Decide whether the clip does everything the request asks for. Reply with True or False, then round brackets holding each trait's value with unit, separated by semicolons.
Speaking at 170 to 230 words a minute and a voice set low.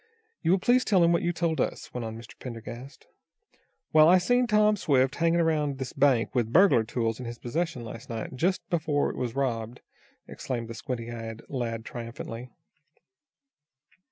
True (175 wpm; 130 Hz)